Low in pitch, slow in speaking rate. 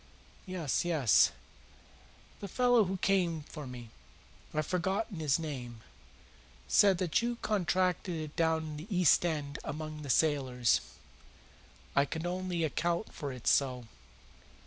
No: medium, 160 Hz; slow, 130 wpm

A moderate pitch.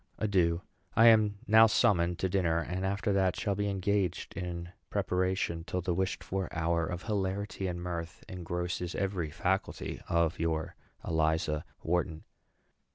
No: very low, 90 Hz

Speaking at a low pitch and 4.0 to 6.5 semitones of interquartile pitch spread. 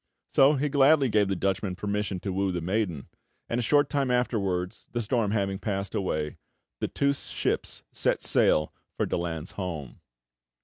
Yes: low, 100 Hz; average, 5.3 semitones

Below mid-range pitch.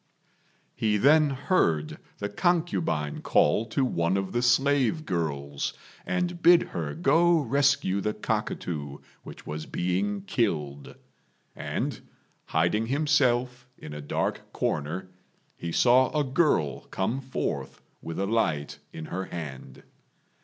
Yes: low, 105 Hz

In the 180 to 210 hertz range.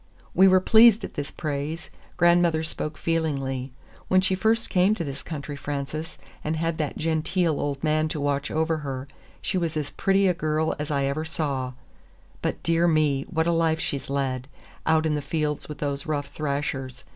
No: medium, 155 Hz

